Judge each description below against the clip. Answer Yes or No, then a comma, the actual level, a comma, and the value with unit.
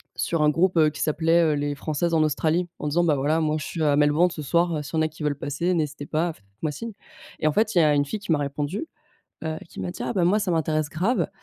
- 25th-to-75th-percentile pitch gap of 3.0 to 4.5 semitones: No, narrow, 2.6 semitones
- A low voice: No, medium, 155 Hz